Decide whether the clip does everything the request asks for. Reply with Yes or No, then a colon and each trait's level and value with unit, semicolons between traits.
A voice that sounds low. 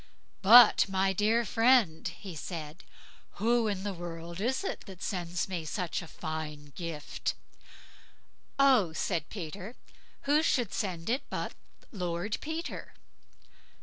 No: high, 190 Hz